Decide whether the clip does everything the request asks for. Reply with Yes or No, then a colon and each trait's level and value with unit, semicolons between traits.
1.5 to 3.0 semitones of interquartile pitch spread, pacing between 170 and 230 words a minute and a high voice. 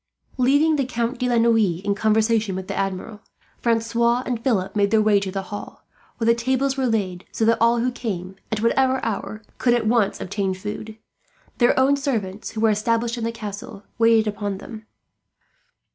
Yes: narrow, 2.6 semitones; average, 190 wpm; high, 225 Hz